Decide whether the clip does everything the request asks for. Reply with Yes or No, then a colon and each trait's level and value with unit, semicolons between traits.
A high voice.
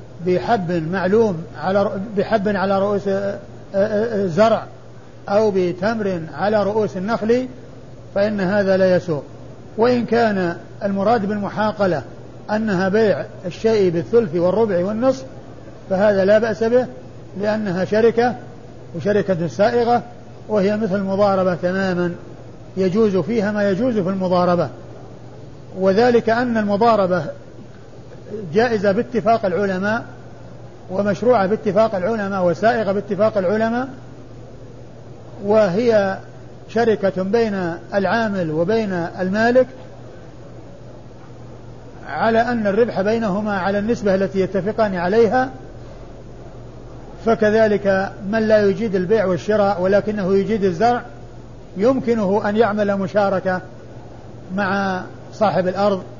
Yes: high, 200 Hz